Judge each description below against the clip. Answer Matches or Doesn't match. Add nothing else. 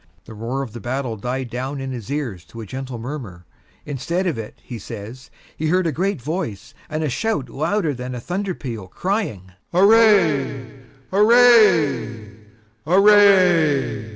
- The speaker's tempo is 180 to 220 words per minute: Doesn't match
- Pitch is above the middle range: Doesn't match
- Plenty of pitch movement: Matches